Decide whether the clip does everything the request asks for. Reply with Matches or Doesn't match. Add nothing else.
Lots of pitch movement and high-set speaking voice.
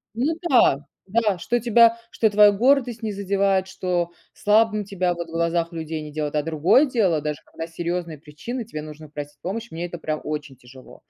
Doesn't match